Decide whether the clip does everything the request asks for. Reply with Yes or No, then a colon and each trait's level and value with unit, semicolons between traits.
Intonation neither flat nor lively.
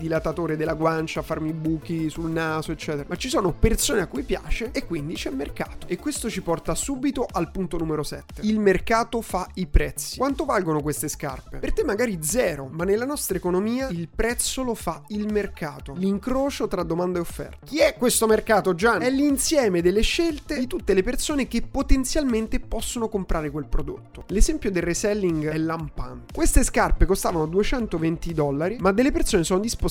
No: wide, 6.9 semitones